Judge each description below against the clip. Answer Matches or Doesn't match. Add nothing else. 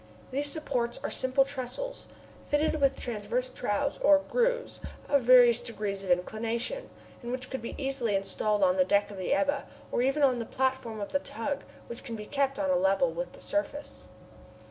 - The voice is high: Matches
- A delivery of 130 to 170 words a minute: Doesn't match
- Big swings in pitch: Doesn't match